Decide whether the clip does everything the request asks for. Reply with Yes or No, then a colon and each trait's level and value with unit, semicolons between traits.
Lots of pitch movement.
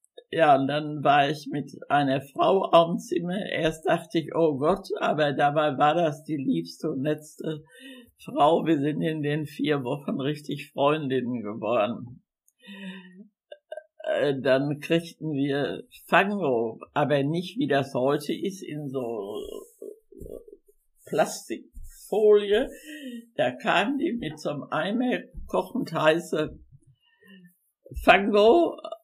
Yes: wide, 7.3 semitones